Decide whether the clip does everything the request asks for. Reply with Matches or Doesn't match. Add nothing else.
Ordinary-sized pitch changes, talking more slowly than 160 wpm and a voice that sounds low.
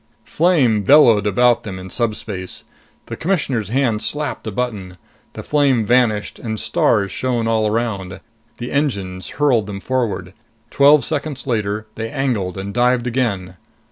Matches